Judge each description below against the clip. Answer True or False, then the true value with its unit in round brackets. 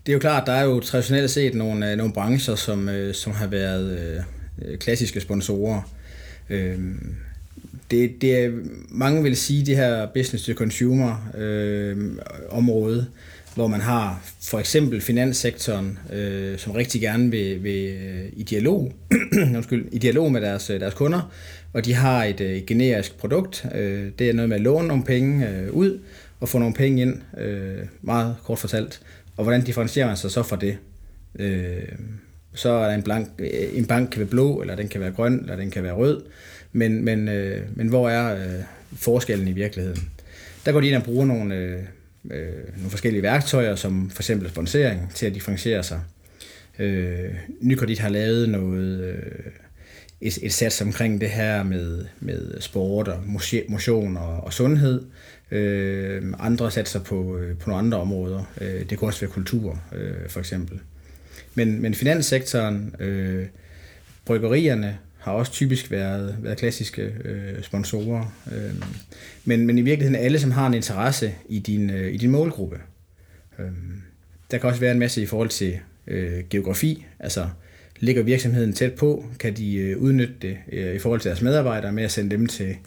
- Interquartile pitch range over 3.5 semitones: True (4.2 semitones)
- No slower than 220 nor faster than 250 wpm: False (160 wpm)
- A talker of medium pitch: False (105 Hz)